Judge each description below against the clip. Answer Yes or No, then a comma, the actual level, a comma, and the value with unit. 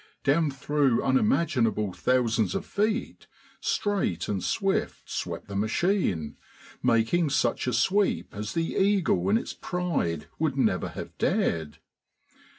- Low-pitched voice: Yes, low, 130 Hz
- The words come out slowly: Yes, slow, 125 wpm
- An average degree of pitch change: No, wide, 9.0 semitones